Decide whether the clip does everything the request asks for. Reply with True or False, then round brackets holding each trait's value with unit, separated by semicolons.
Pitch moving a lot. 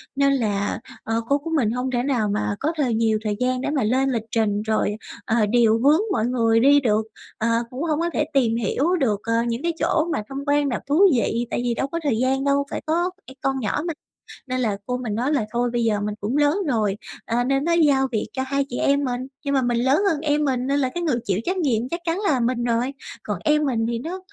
False (3.8 semitones)